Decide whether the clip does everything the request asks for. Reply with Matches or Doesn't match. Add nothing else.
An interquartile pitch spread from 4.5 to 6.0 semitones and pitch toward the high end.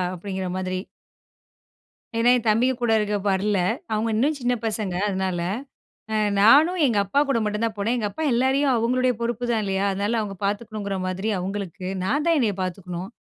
Doesn't match